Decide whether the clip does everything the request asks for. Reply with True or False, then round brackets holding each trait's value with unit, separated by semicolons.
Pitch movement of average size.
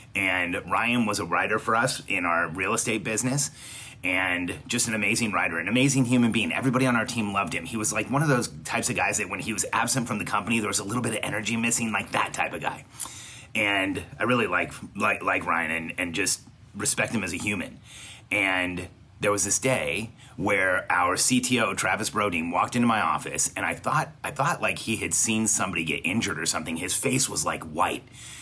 True (3.5 semitones)